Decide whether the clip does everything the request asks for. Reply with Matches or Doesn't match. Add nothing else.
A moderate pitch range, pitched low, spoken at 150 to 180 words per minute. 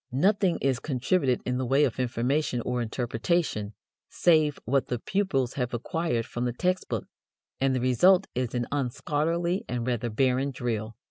Matches